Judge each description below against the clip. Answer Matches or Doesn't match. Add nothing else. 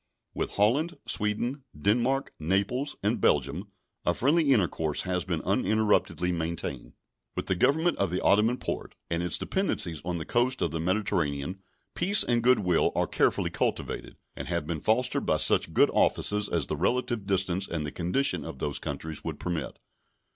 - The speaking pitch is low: Matches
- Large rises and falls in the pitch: Matches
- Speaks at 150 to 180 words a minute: Matches